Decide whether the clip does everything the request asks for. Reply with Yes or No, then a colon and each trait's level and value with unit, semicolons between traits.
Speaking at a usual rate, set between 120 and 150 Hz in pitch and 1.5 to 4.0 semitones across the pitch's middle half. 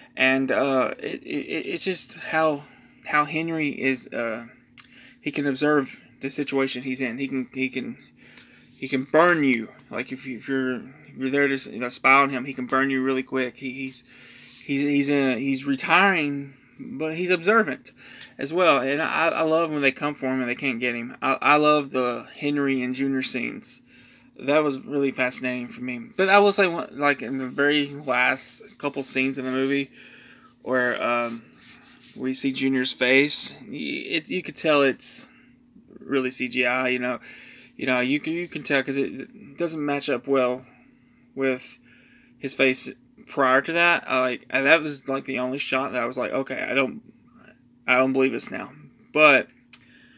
Yes: average, 190 wpm; low, 135 Hz; narrow, 2.6 semitones